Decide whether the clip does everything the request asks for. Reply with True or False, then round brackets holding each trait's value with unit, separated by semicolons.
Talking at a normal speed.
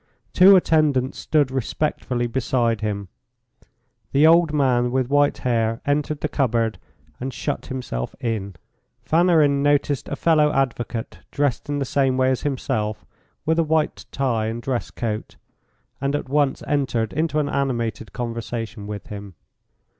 True (145 wpm)